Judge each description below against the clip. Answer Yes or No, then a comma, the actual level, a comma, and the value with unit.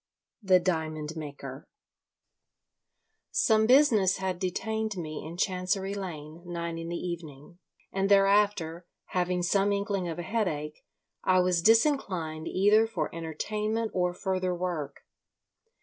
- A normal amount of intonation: Yes, average, 3.4 semitones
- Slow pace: Yes, slow, 125 wpm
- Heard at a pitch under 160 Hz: No, medium, 180 Hz